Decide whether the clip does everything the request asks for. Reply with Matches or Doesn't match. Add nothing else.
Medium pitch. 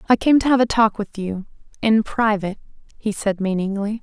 Doesn't match